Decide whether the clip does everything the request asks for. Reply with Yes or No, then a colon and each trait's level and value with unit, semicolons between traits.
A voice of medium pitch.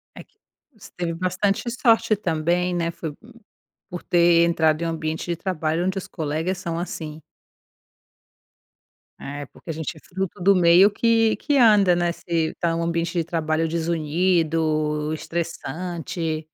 Yes: medium, 170 Hz